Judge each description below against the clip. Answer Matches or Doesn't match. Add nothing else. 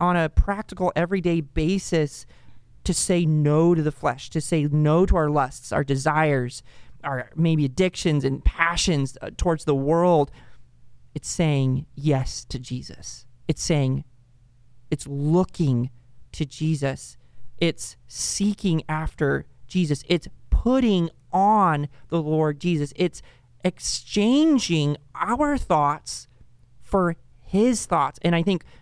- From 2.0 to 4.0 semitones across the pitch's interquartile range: Doesn't match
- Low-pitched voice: Doesn't match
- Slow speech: Matches